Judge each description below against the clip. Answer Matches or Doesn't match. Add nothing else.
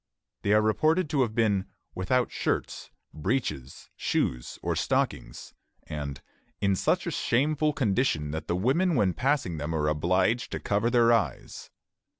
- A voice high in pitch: Doesn't match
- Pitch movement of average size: Doesn't match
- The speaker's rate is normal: Matches